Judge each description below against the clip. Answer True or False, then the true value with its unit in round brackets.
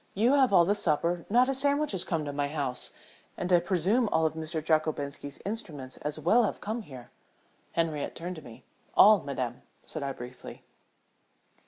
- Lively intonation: True (6.1 semitones)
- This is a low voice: False (165 Hz)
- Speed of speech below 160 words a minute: False (180 wpm)